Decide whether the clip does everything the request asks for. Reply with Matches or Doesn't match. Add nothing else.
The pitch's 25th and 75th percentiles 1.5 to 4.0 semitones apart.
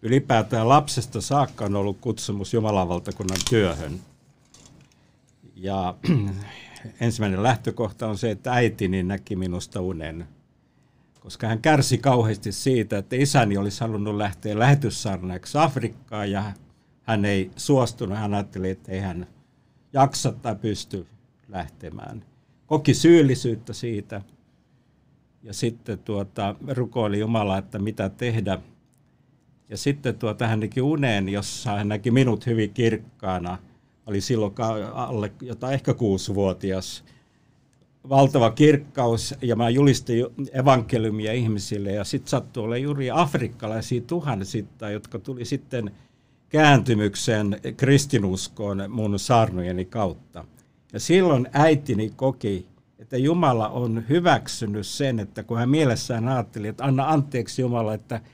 Doesn't match